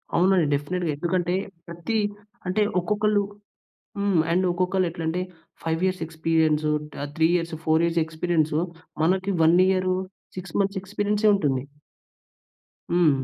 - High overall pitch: No, medium, 175 Hz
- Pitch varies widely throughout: No, average, 2.8 semitones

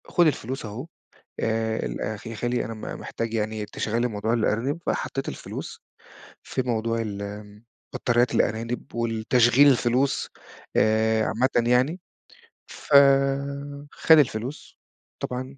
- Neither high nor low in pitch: No, low, 115 Hz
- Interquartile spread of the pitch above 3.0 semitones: No, narrow, 2.5 semitones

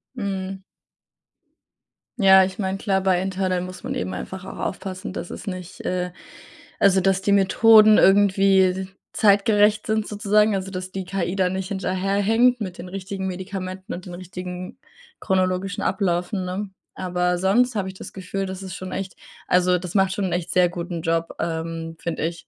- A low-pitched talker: No, high, 190 Hz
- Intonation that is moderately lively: No, narrow, 1.3 semitones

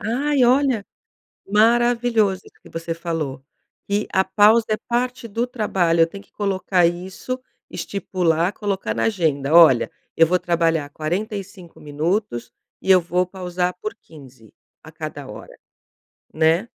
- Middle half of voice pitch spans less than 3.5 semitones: No, average, 4.6 semitones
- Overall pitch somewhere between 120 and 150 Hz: No, medium, 185 Hz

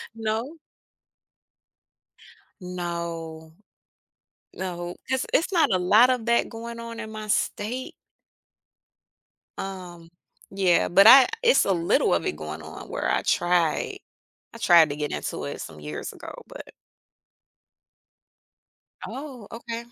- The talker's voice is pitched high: Yes, high, 195 Hz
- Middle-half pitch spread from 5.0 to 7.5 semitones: Yes, wide, 5.4 semitones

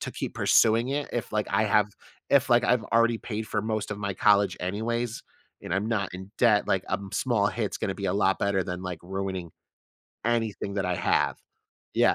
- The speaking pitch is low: Yes, low, 105 Hz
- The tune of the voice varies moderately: Yes, average, 3.0 semitones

